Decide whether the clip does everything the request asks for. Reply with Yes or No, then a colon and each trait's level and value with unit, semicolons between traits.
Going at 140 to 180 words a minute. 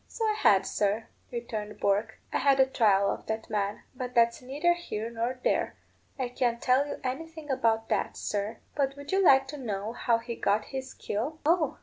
No: average, 200 wpm